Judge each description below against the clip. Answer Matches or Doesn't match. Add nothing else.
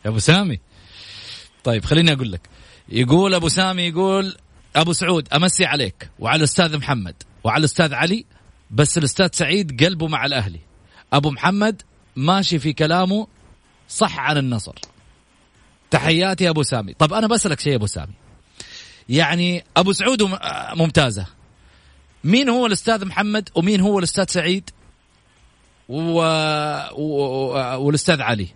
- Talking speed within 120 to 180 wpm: Matches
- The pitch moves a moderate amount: Doesn't match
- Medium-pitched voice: Matches